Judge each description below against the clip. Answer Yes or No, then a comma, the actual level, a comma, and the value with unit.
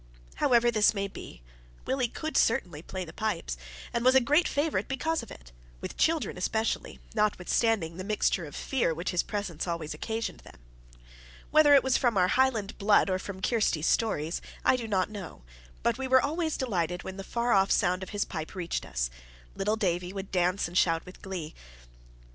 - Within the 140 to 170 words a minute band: No, average, 190 wpm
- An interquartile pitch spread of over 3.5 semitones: Yes, average, 5.0 semitones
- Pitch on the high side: Yes, high, 200 Hz